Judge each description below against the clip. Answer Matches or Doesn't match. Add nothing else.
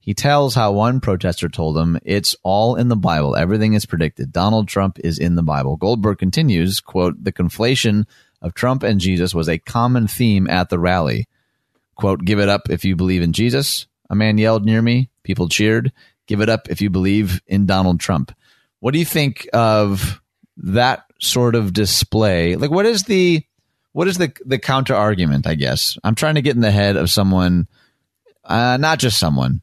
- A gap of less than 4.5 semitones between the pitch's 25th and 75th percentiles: Doesn't match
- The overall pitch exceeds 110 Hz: Doesn't match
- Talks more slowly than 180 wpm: Doesn't match